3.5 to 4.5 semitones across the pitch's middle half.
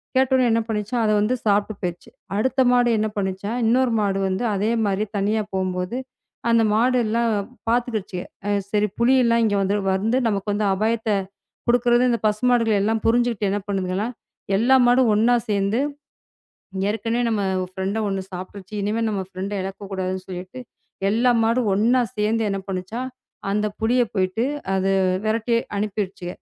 No: average, 3.0 semitones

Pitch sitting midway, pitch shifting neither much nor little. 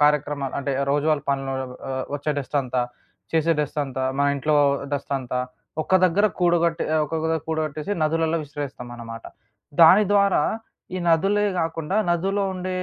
Yes: medium, 155 Hz; average, 3.1 semitones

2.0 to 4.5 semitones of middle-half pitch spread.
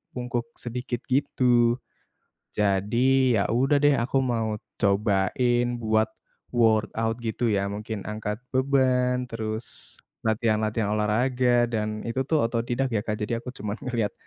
Yes: average, 2.7 semitones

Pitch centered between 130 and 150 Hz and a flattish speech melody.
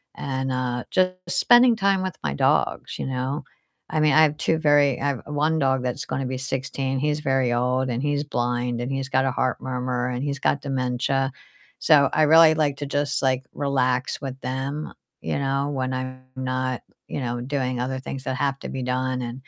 Yes: low, 135 Hz; narrow, 2.1 semitones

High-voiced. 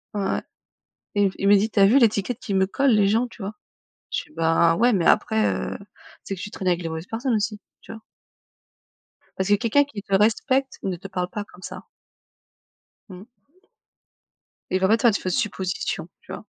Yes: high, 205 Hz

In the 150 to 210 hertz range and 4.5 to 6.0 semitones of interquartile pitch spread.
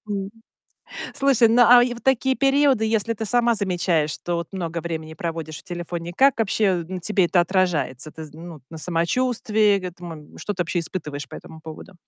Yes: medium, 185 Hz; average, 5.1 semitones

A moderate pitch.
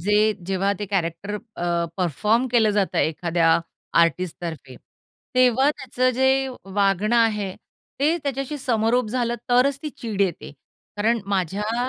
No: high, 210 Hz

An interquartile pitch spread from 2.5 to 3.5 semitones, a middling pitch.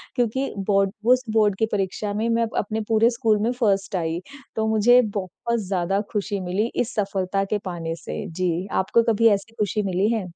No: average, 3.0 semitones; high, 210 Hz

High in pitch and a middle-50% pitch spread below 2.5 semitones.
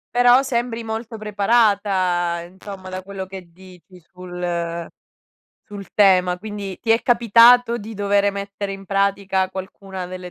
No: high, 195 Hz; average, 2.9 semitones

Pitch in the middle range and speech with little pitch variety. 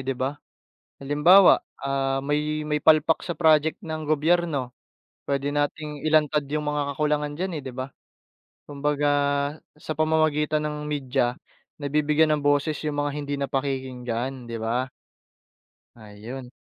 Yes: medium, 145 Hz; narrow, 2.2 semitones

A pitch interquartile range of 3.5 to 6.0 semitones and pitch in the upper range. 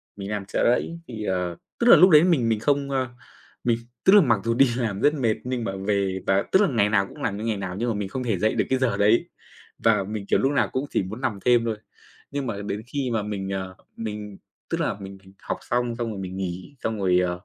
No: average, 4.4 semitones; low, 110 Hz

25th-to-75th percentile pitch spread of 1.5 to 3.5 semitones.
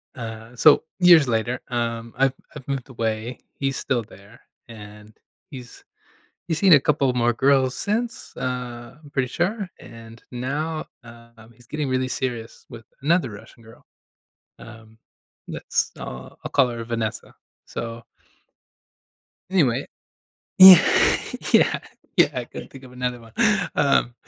Yes: average, 3.1 semitones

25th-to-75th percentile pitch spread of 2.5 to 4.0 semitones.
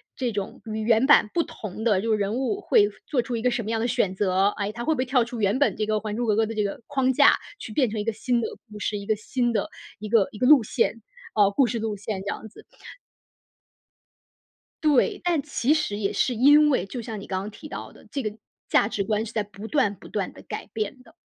Yes: average, 3.5 semitones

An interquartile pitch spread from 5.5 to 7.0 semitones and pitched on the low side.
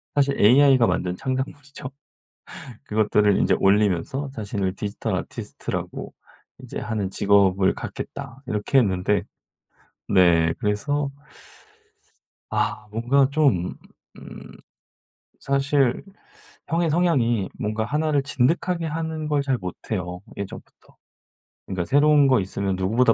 Yes: wide, 6.1 semitones; low, 120 Hz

